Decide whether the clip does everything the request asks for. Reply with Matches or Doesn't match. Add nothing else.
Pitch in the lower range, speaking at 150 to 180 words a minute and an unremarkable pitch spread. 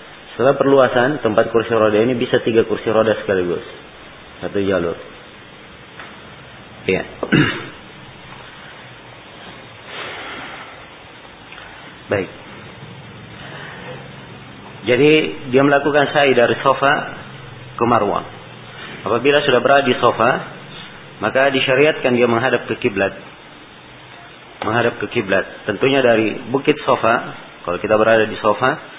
Doesn't match